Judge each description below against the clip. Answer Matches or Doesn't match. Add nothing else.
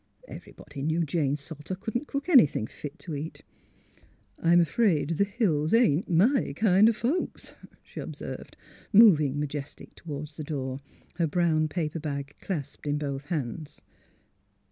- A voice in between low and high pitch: Matches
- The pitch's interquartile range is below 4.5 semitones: Doesn't match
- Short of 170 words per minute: Matches